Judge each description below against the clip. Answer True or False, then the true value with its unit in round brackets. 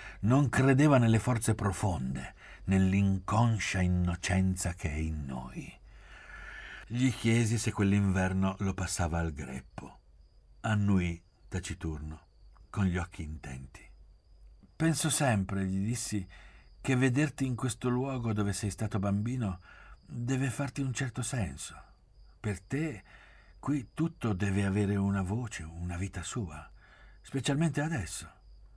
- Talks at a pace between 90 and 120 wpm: True (115 wpm)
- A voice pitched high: False (100 Hz)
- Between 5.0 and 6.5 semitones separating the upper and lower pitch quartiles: True (5.3 semitones)